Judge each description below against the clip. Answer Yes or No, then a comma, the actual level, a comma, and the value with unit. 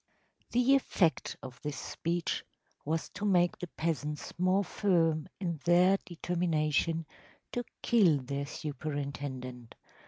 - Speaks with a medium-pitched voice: Yes, medium, 165 Hz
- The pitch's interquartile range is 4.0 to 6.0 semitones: No, average, 3.6 semitones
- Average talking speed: No, slow, 120 wpm